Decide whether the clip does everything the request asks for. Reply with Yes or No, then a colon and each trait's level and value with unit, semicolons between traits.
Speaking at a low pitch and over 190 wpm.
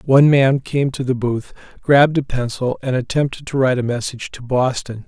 Yes: low, 130 Hz; average, 200 wpm